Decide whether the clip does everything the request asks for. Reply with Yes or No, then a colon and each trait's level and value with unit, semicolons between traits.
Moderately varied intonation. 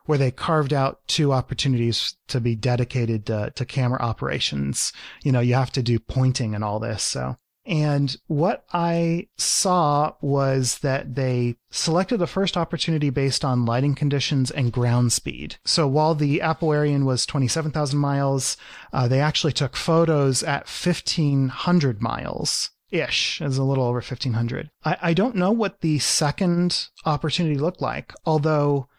Yes: average, 3.8 semitones